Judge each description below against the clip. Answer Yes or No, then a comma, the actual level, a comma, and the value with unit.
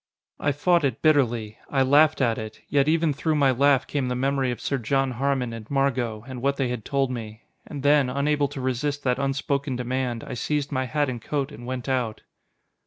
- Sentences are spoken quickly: Yes, fast, 210 wpm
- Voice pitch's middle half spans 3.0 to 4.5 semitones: No, narrow, 2.5 semitones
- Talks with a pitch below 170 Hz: Yes, low, 135 Hz